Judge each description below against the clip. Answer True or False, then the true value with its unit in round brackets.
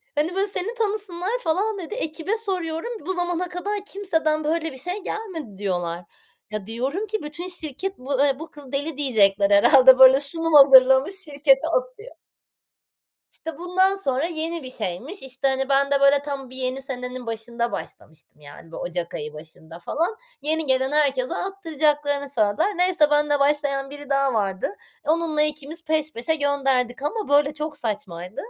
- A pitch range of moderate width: True (4.7 semitones)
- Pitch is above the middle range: True (290 Hz)